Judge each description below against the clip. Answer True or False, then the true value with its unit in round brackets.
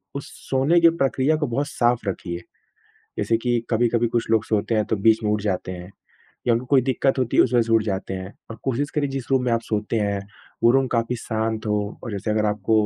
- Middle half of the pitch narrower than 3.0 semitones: False (3.4 semitones)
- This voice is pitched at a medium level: False (115 Hz)